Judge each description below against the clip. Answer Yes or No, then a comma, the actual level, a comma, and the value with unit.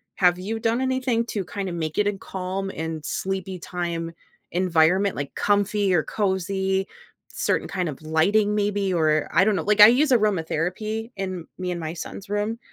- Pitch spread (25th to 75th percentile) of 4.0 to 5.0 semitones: No, average, 3.2 semitones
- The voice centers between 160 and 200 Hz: Yes, high, 190 Hz